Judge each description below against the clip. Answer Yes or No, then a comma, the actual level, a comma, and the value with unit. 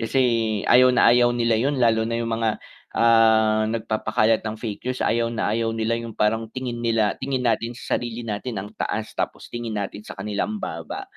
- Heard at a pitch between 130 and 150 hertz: No, low, 115 Hz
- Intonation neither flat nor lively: No, narrow, 1.5 semitones